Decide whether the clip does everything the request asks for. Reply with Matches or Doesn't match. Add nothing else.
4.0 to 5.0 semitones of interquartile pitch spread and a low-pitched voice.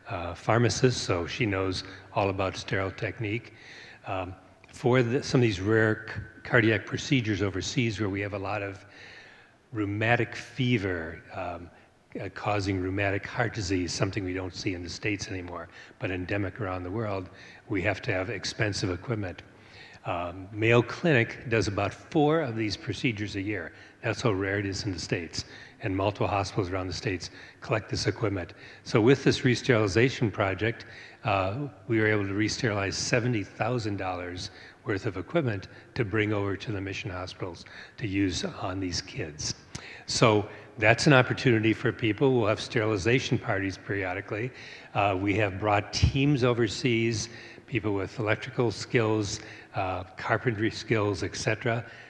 Doesn't match